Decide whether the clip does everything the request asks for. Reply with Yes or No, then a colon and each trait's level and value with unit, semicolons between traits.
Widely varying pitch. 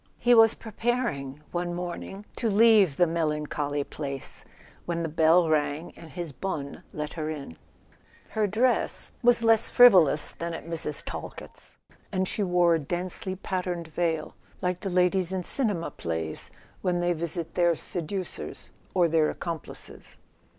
No: average, 3.5 semitones